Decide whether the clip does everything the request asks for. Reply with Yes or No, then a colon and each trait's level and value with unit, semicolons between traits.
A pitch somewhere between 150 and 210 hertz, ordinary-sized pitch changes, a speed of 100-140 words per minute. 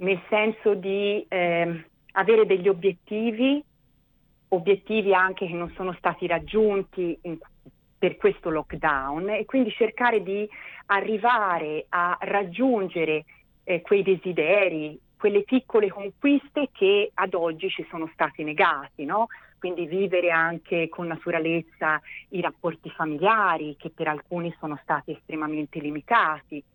Yes: medium, 185 Hz; average, 4.2 semitones; average, 120 wpm